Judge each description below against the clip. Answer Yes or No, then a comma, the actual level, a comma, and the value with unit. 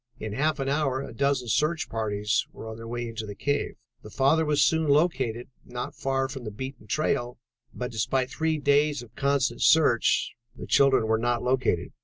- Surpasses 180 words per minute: Yes, average, 190 wpm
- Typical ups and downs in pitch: Yes, average, 3.8 semitones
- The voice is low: Yes, low, 130 Hz